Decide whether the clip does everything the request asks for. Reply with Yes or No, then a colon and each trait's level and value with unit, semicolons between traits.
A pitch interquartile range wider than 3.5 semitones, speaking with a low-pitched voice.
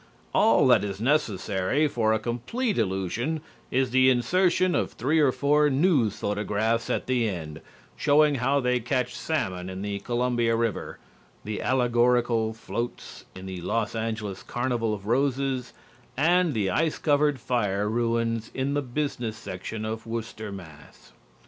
Yes: average, 4.2 semitones; low, 120 Hz